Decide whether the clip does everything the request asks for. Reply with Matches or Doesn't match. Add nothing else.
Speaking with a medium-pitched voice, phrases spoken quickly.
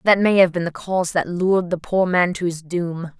Matches